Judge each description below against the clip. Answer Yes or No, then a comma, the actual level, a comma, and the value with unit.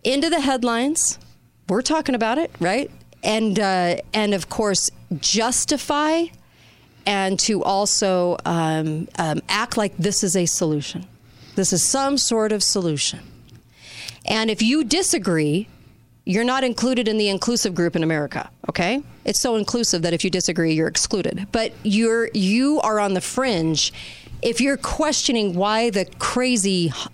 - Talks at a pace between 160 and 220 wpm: No, average, 150 wpm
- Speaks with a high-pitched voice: Yes, high, 205 Hz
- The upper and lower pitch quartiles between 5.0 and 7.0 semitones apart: Yes, wide, 5.4 semitones